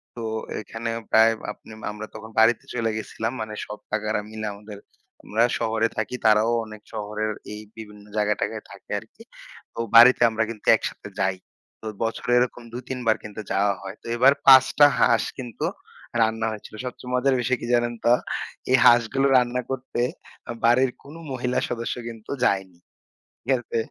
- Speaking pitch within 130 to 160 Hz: No, low, 115 Hz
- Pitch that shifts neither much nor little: No, narrow, 2.2 semitones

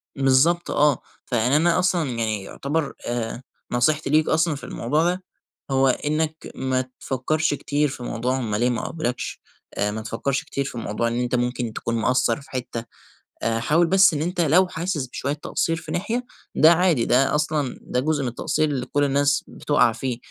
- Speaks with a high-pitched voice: No, medium, 140 Hz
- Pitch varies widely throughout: No, average, 4.3 semitones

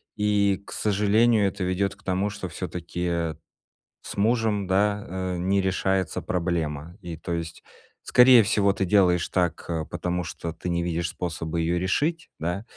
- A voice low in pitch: Yes, very low, 95 Hz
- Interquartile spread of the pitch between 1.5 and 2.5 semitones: No, average, 2.9 semitones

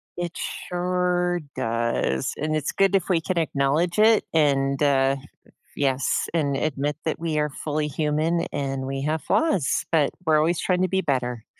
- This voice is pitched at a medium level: Yes, medium, 155 Hz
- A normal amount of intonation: Yes, average, 4.1 semitones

